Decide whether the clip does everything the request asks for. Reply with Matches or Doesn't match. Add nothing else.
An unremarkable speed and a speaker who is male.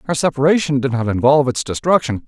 Matches